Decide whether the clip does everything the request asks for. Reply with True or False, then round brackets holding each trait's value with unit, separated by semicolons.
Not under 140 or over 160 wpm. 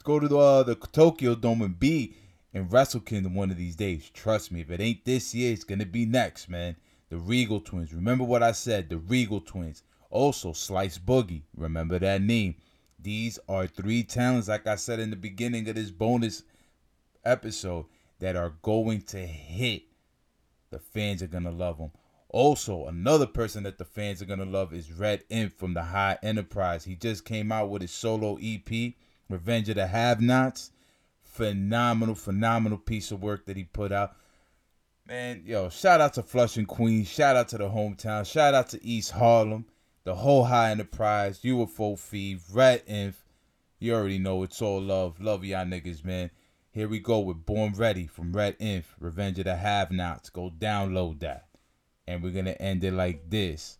False (190 wpm)